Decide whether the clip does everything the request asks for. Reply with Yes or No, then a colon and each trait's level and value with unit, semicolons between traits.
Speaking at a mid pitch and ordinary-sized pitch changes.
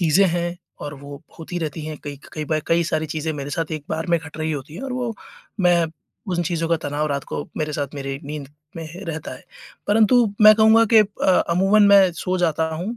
Yes: medium, 165 Hz; average, 3.8 semitones